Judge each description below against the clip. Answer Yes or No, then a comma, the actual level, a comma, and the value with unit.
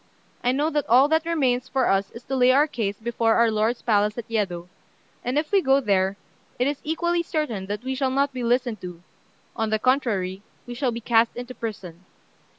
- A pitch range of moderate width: Yes, average, 4.1 semitones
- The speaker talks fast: Yes, fast, 210 wpm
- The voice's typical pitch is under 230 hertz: No, high, 240 Hz